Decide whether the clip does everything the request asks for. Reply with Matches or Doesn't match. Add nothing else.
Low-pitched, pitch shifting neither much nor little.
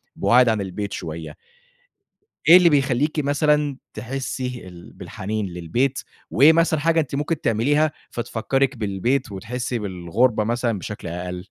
Doesn't match